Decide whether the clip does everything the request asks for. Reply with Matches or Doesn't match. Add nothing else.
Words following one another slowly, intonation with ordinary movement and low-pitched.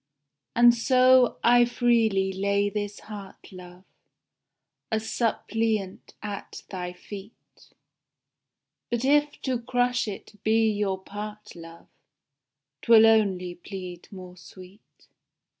Doesn't match